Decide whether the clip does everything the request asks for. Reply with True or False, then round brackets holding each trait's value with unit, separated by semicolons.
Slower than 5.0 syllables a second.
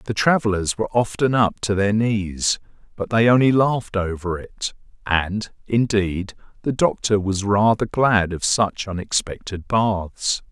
True (4.1 syllables/s)